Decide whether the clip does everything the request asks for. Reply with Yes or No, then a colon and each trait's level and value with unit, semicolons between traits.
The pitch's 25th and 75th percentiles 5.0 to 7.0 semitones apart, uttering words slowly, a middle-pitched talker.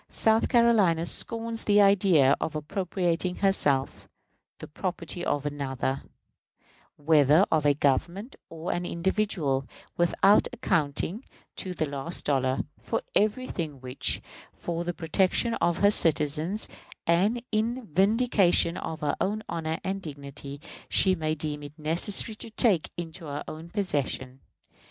Yes: average, 5.3 semitones; slow, 130 wpm; medium, 170 Hz